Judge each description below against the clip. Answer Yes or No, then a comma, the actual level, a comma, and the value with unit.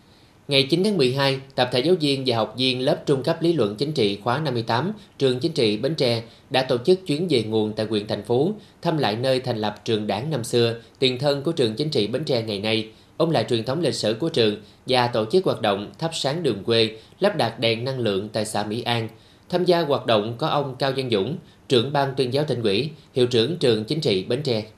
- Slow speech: No, average, 245 wpm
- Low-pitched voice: Yes, low, 125 Hz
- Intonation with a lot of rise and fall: No, average, 4.7 semitones